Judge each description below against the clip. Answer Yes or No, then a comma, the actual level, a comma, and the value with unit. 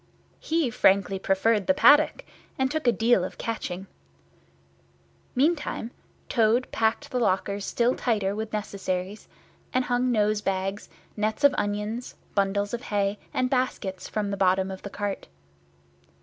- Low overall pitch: No, high, 215 Hz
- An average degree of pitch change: Yes, average, 3.9 semitones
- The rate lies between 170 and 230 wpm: No, slow, 135 wpm